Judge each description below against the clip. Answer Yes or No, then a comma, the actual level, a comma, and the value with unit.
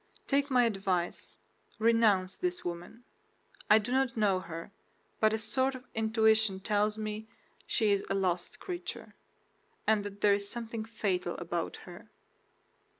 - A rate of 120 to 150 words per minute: Yes, average, 145 wpm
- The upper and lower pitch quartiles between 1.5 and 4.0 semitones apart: Yes, average, 3.0 semitones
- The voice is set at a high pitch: Yes, high, 215 Hz